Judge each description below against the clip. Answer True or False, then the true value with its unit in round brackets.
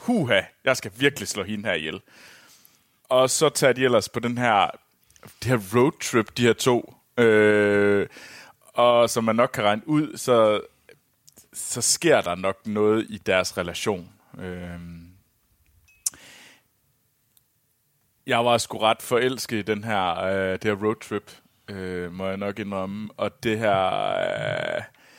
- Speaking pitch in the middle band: False (110 Hz)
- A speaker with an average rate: False (135 wpm)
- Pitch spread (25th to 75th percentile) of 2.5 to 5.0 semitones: True (3.4 semitones)